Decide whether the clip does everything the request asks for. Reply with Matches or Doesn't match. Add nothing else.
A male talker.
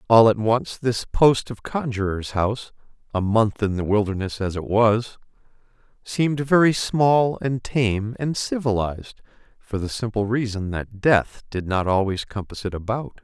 Matches